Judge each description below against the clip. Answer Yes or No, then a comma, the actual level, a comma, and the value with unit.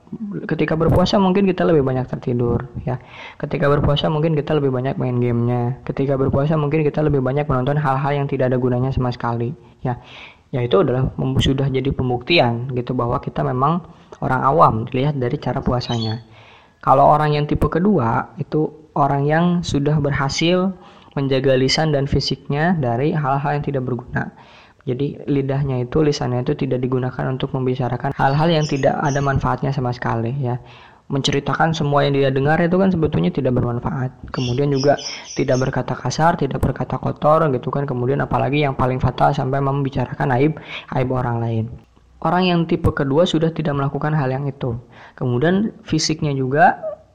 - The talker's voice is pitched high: No, medium, 140 Hz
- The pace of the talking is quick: Yes, fast, 160 wpm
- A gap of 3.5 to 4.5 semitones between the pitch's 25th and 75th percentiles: No, average, 3.0 semitones